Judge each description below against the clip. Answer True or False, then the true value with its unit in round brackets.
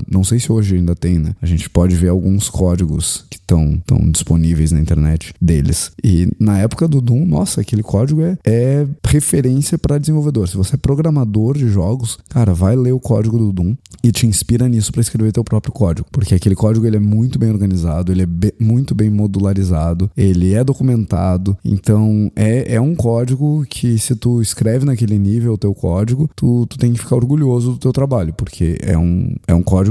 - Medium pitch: False (110 Hz)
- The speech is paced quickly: True (200 wpm)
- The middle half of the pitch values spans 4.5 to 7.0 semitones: True (5.1 semitones)